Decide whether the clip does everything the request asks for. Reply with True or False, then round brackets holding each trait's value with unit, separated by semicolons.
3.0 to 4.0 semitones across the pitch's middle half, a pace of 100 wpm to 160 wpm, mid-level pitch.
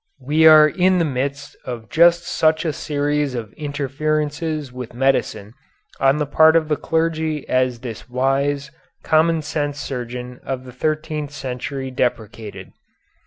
True (3.5 semitones; 140 wpm; 145 Hz)